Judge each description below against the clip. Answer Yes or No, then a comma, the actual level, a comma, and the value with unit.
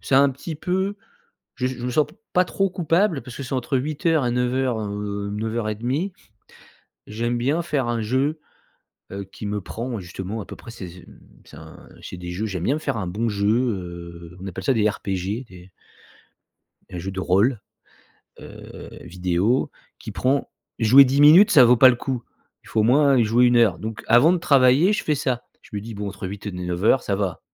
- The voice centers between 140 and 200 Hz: No, low, 120 Hz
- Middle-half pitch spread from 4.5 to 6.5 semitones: Yes, average, 5.2 semitones